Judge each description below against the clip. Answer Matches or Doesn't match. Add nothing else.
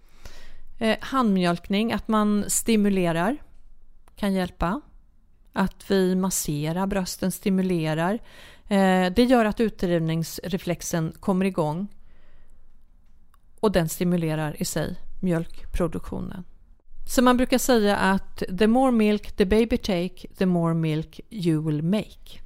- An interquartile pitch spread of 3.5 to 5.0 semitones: Matches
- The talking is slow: Matches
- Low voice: Doesn't match